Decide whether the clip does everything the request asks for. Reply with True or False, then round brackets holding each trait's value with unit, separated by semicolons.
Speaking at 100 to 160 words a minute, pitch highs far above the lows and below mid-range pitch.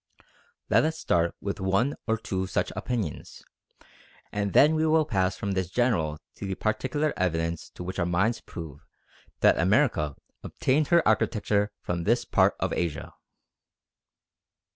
True (145 wpm; 5.8 semitones; 100 Hz)